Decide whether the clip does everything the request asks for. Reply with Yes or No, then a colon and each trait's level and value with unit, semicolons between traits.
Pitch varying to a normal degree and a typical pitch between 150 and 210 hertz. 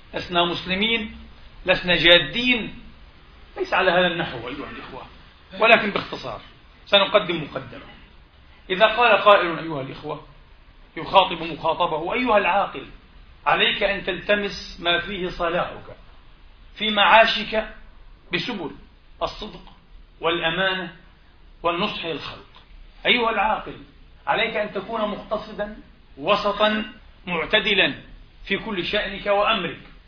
Yes: average, 3.9 semitones; high, 190 Hz